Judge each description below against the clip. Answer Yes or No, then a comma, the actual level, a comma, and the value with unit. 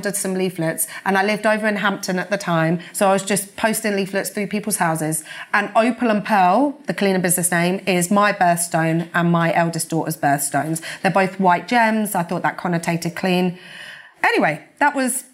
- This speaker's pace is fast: No, average, 190 wpm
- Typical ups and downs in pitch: Yes, average, 3.3 semitones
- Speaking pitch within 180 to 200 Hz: Yes, medium, 185 Hz